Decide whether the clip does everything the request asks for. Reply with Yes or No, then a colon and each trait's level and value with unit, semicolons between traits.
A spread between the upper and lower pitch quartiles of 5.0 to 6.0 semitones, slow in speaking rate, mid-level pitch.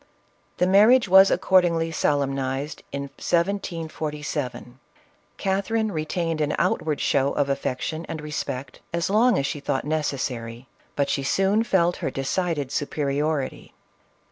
No: average, 4.5 semitones; slow, 120 wpm; medium, 155 Hz